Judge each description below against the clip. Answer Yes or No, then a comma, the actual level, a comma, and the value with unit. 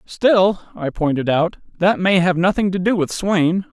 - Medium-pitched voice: Yes, medium, 180 Hz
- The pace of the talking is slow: No, average, 190 wpm